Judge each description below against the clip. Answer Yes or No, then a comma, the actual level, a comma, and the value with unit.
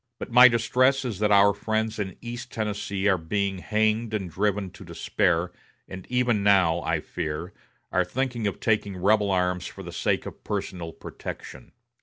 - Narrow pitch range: No, average, 3.4 semitones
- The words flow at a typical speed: Yes, average, 170 wpm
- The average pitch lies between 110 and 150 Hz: No, low, 100 Hz